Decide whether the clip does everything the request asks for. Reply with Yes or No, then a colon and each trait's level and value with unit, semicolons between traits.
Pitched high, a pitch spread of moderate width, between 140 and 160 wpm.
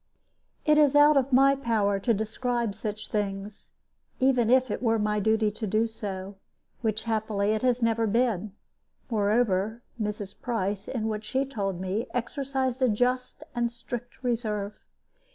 Yes: high, 225 Hz; average, 3.1 semitones; average, 150 wpm